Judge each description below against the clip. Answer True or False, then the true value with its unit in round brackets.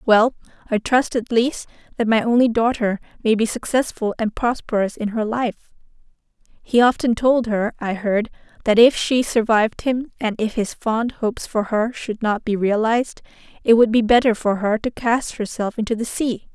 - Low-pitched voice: False (225 Hz)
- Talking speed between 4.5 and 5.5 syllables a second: True (4.9 syllables/s)